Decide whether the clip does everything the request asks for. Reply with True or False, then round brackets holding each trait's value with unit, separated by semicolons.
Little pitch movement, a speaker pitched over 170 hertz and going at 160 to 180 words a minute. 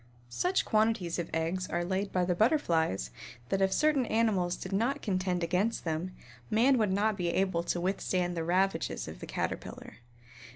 False (3.8 semitones; 185 Hz; 170 wpm)